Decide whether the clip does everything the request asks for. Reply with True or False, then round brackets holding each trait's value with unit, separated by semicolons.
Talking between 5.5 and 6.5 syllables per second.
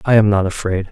True (6.3 syllables/s)